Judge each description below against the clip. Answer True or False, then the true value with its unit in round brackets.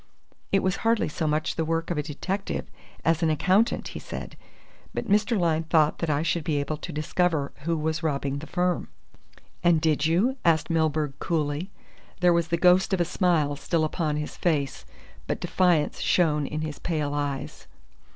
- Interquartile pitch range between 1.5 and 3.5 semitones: True (2.8 semitones)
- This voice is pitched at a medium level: True (160 Hz)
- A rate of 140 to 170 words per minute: False (180 wpm)